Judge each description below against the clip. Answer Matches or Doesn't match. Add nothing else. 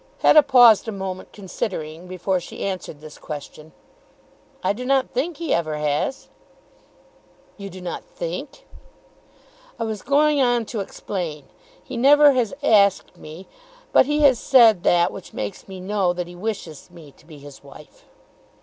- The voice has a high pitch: Matches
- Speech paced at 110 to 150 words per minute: Doesn't match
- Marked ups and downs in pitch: Matches